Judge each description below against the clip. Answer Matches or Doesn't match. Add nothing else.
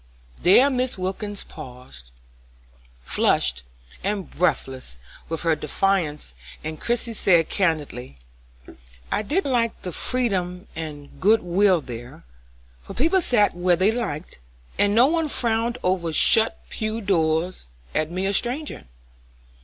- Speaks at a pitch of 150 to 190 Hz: Matches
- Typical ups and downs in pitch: Doesn't match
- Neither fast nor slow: Doesn't match